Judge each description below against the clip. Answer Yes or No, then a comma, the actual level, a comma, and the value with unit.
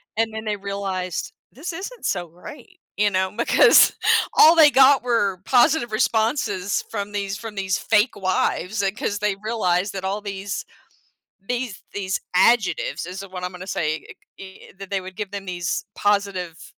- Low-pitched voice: No, high, 200 Hz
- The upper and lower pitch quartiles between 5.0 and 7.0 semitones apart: No, average, 3.2 semitones